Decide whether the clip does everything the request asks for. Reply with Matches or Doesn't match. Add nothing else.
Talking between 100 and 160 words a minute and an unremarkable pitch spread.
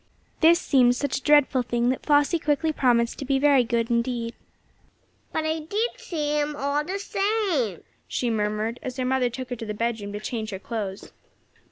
Doesn't match